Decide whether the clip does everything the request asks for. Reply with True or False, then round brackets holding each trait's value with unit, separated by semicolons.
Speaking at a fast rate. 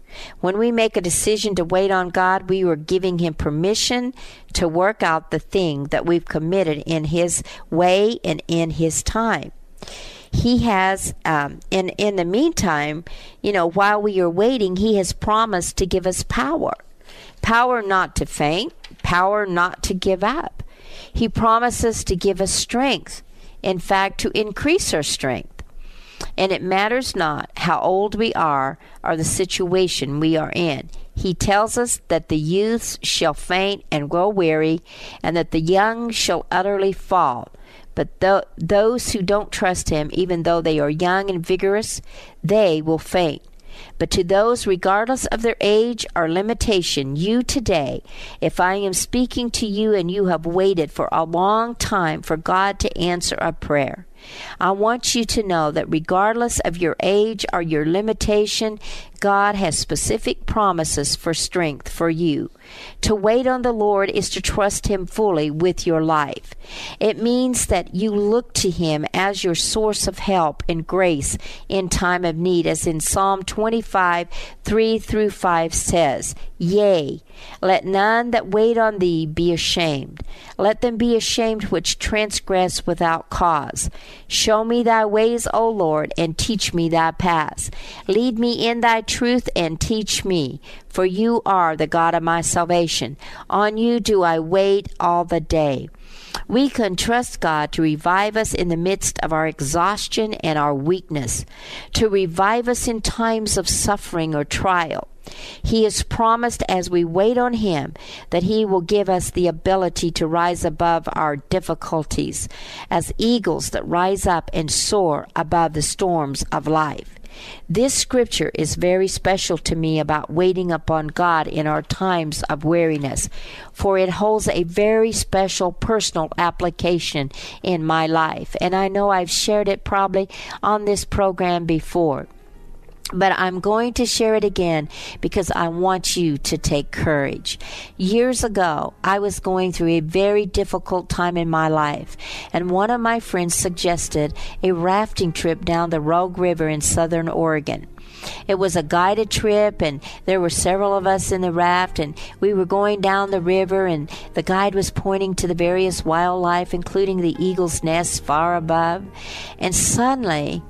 False (165 wpm)